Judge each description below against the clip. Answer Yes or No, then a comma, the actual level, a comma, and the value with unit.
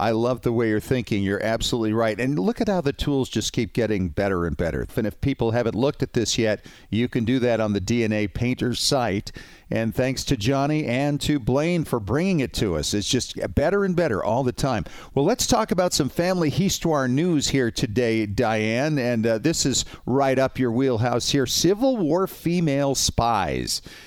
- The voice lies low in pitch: Yes, low, 125 Hz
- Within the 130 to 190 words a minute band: No, fast, 205 wpm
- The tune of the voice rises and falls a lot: No, average, 4.3 semitones